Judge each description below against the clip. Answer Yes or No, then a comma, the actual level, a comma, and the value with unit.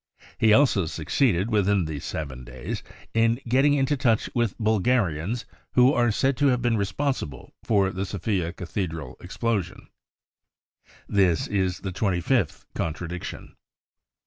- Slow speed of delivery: Yes, slow, 130 wpm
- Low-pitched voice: Yes, low, 100 Hz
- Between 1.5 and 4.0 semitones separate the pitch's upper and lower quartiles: No, wide, 5.5 semitones